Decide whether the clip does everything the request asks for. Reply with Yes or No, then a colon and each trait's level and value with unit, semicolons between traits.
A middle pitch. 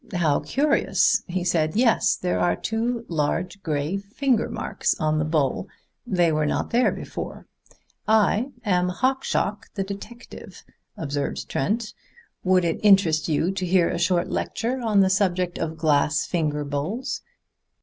Yes: medium, 180 Hz